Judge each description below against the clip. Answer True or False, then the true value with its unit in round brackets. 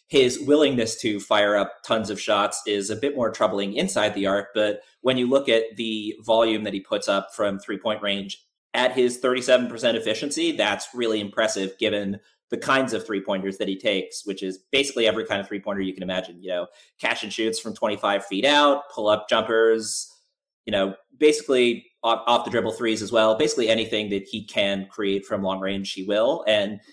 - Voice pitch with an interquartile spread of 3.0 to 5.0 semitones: True (3.9 semitones)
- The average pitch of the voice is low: True (110 Hz)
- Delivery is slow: False (205 wpm)